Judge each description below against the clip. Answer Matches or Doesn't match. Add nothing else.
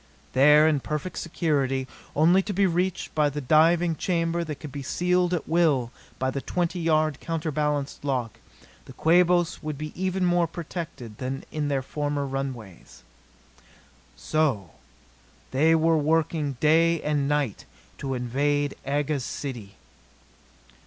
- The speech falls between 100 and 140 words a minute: Matches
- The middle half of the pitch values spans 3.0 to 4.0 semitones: Matches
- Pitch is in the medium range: Matches